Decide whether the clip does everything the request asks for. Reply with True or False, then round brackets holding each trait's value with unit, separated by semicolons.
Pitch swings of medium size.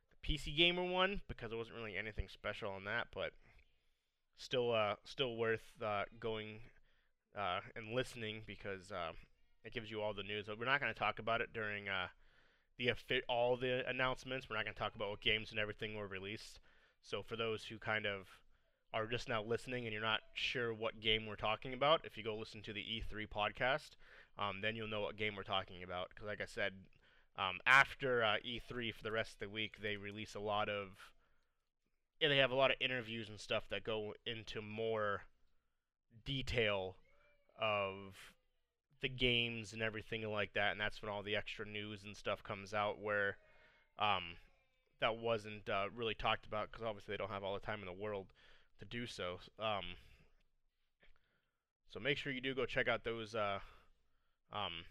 False (2.3 semitones)